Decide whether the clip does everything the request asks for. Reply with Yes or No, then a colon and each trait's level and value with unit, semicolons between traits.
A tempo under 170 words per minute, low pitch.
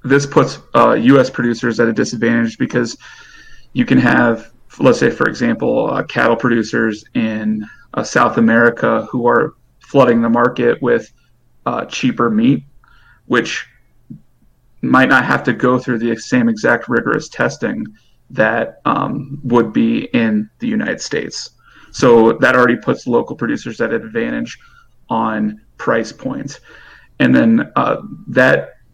Yes: average, 140 wpm; low, 120 Hz